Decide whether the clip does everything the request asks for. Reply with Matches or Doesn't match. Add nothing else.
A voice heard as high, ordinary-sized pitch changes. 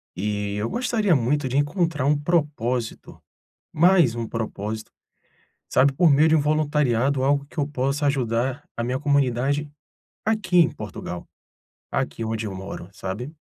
Doesn't match